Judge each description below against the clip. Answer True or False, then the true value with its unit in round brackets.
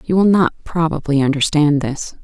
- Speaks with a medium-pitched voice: True (155 Hz)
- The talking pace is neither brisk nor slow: True (160 wpm)